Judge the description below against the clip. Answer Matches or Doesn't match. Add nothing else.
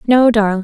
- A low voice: Doesn't match